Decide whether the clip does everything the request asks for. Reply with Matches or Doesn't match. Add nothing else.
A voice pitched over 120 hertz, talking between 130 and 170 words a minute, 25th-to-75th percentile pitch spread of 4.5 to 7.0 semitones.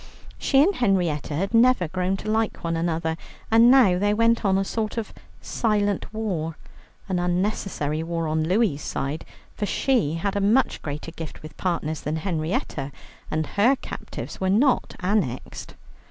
Matches